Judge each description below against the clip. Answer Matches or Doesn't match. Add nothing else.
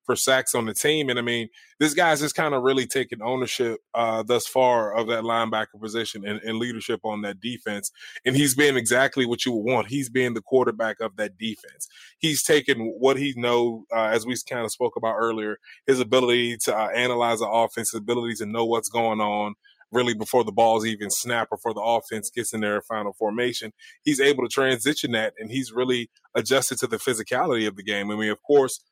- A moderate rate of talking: Doesn't match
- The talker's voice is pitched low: Matches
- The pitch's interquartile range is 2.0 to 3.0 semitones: Matches